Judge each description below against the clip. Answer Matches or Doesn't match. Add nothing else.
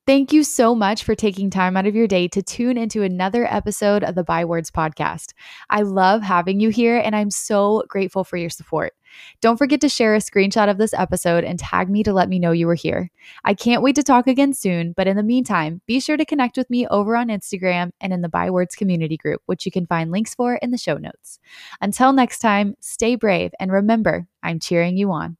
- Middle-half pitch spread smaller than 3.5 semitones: Doesn't match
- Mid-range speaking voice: Doesn't match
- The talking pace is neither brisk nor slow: Doesn't match